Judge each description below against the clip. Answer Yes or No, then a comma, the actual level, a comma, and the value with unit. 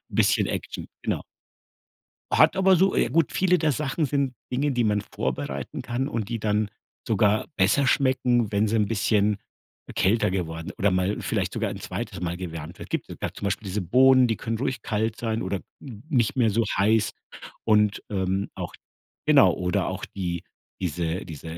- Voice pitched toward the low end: Yes, low, 105 Hz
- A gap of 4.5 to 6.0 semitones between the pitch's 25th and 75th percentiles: Yes, average, 4.9 semitones